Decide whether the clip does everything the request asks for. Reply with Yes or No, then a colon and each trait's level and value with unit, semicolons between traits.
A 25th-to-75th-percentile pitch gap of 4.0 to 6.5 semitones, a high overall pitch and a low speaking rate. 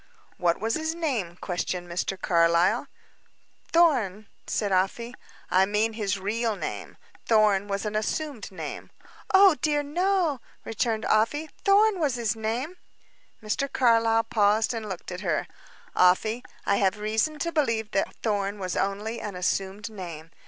No: average, 4.6 semitones; high, 215 Hz; average, 145 wpm